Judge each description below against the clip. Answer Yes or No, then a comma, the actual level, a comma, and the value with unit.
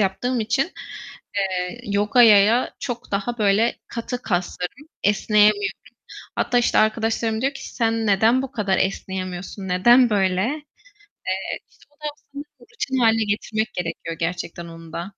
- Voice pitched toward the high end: Yes, high, 220 Hz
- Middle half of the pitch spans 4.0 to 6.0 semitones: Yes, average, 4.3 semitones